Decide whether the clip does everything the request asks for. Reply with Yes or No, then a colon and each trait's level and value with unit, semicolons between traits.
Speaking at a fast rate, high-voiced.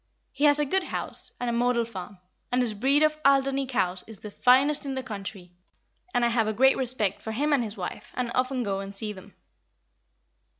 Yes: fast, 215 wpm; high, 245 Hz